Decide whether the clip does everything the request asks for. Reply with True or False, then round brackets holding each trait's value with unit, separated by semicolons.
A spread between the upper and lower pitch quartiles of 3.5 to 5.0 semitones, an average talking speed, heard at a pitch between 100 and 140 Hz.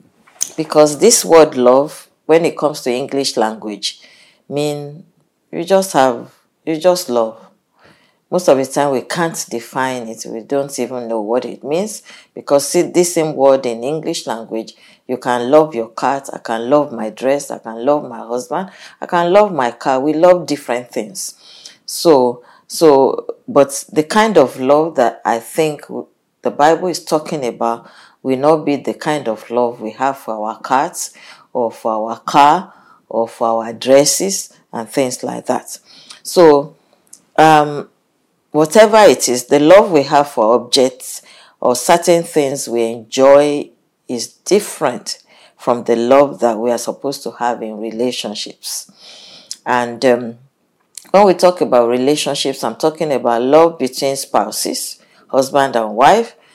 True (4.3 semitones; 155 wpm; 135 Hz)